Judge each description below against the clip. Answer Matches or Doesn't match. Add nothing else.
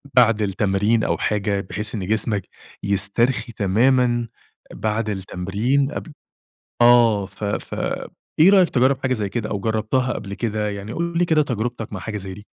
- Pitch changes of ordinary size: Matches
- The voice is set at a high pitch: Doesn't match